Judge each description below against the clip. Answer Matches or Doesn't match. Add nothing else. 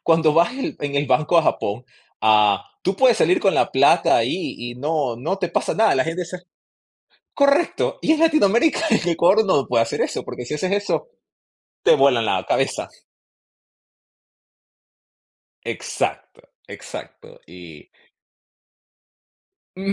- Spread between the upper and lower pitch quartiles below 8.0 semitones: Doesn't match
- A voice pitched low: Doesn't match